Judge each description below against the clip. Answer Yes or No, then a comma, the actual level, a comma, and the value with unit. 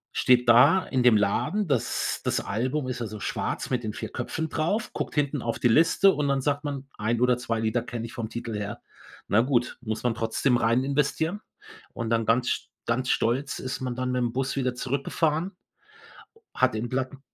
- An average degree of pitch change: Yes, average, 3.1 semitones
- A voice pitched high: No, low, 125 Hz